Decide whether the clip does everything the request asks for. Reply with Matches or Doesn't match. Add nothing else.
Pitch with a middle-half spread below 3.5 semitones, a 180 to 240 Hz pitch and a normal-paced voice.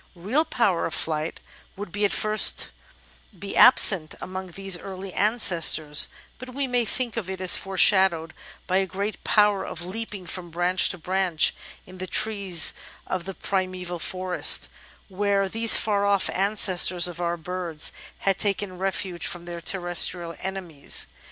Matches